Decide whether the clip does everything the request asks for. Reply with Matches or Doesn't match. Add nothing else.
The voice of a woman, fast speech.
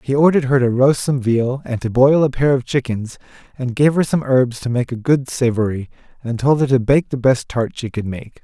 Doesn't match